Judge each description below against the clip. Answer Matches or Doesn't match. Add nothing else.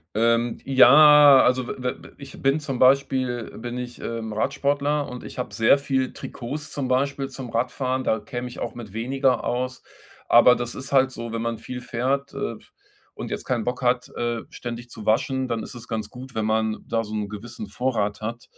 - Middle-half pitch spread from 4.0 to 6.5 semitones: Doesn't match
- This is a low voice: Matches